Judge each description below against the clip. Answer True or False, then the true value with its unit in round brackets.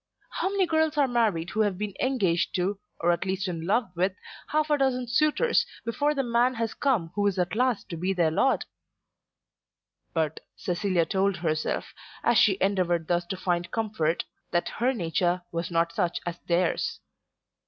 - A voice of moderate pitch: False (195 Hz)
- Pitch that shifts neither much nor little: False (5.7 semitones)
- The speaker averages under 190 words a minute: True (175 wpm)